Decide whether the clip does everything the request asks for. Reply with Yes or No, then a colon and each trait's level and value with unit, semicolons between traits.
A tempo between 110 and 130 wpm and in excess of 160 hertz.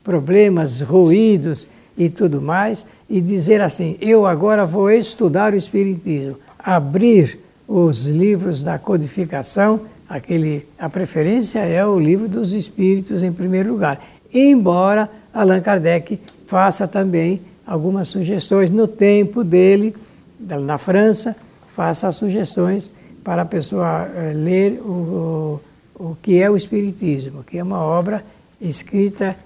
Yes: slow, 120 wpm; high, 190 Hz